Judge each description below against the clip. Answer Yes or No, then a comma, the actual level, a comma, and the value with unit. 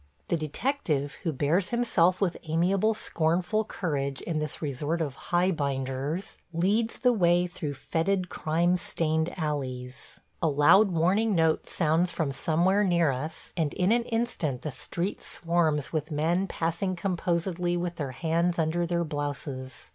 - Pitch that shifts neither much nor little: Yes, average, 3.1 semitones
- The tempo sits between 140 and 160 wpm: Yes, average, 145 wpm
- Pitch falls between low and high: Yes, medium, 170 Hz